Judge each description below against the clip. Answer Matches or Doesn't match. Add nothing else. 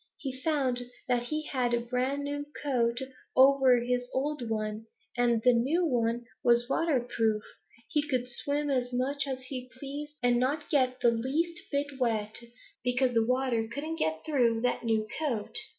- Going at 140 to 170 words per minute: Matches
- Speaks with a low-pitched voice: Doesn't match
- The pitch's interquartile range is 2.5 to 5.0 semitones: Matches